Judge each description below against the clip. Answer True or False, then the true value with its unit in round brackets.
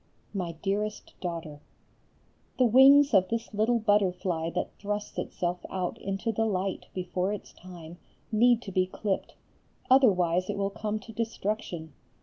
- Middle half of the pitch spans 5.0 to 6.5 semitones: False (3.3 semitones)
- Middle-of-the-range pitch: False (195 Hz)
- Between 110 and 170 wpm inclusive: True (140 wpm)